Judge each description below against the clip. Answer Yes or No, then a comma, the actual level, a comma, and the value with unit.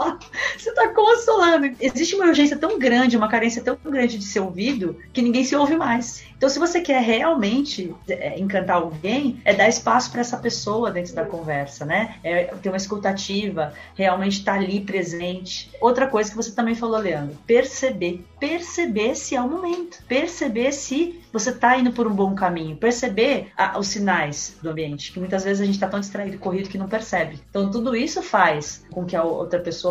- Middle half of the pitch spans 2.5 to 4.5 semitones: No, wide, 5.6 semitones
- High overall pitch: Yes, high, 220 Hz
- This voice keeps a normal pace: No, fast, 190 wpm